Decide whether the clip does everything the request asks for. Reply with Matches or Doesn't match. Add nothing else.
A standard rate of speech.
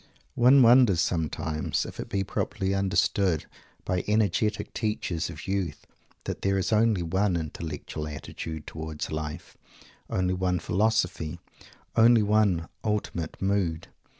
Doesn't match